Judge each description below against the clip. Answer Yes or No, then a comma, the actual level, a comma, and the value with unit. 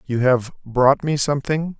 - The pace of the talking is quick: No, average, 165 wpm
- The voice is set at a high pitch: No, low, 135 Hz